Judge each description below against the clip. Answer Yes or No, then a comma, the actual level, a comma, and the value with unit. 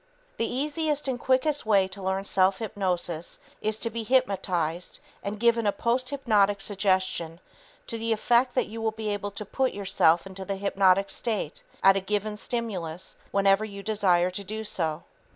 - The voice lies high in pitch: Yes, high, 205 Hz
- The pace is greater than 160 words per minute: Yes, average, 170 wpm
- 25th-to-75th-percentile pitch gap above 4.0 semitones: No, average, 3.3 semitones